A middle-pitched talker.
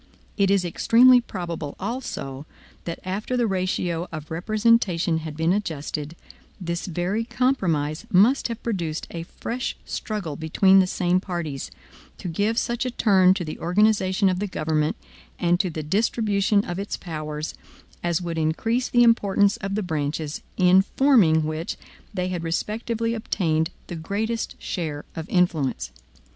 Yes: medium, 180 Hz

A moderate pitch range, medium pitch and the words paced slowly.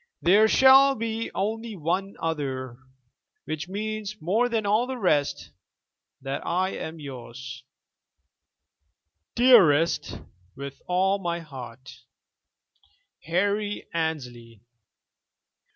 No: wide, 7.3 semitones; medium, 175 Hz; slow, 90 wpm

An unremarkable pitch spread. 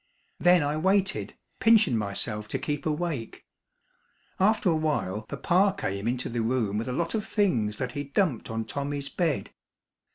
No: wide, 7.8 semitones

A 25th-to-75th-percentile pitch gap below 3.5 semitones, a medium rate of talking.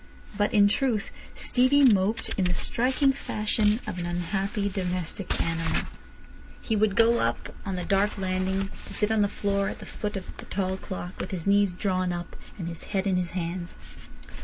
Yes: narrow, 2.5 semitones; average, 185 wpm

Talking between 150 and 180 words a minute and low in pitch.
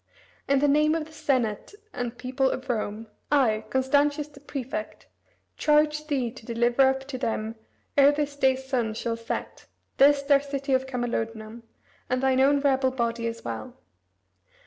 No: average, 160 wpm; very high, 265 Hz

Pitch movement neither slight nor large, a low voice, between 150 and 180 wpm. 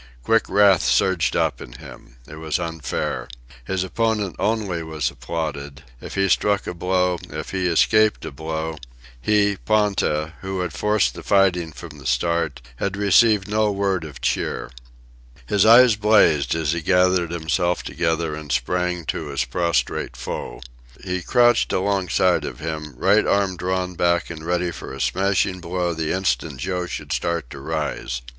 Yes: average, 3.7 semitones; very low, 90 Hz; average, 160 wpm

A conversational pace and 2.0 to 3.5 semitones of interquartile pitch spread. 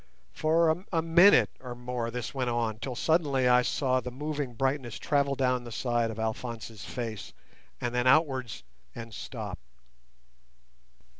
Yes: average, 145 wpm; average, 3.2 semitones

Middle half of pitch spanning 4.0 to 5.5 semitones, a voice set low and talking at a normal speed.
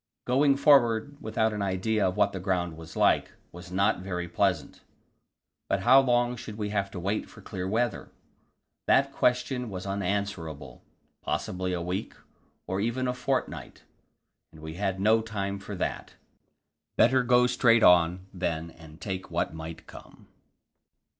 Yes: average, 4.4 semitones; low, 100 Hz; average, 155 wpm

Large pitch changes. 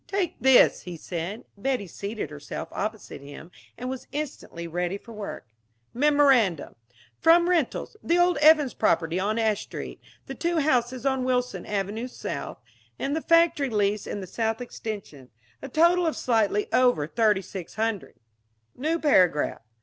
Yes: wide, 6.4 semitones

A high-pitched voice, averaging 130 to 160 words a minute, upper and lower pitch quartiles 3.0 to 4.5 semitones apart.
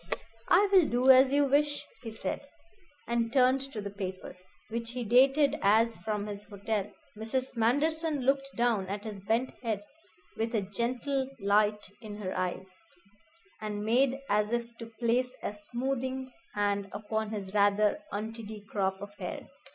Yes: high, 225 Hz; average, 155 wpm; average, 4.0 semitones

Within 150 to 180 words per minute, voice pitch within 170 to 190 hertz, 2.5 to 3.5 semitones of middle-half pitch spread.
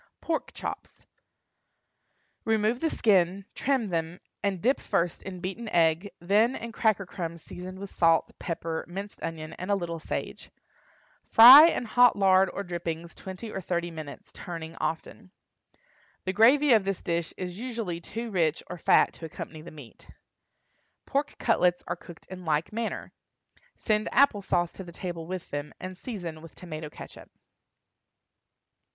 No: average, 155 wpm; medium, 185 Hz; average, 4.3 semitones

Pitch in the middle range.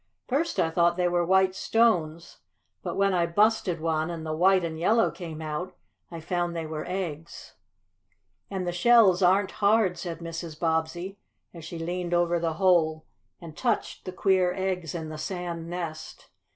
Yes: medium, 175 Hz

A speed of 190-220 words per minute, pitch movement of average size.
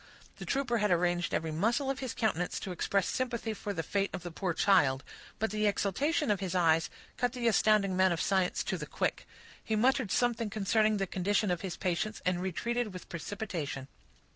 Yes: average, 195 wpm; average, 3.9 semitones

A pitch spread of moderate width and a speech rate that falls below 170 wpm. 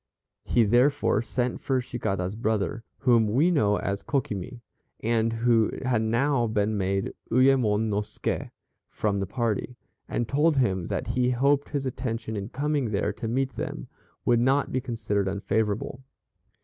Yes: average, 3.6 semitones; average, 150 wpm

